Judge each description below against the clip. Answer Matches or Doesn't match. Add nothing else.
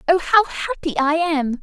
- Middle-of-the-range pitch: Doesn't match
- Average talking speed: Matches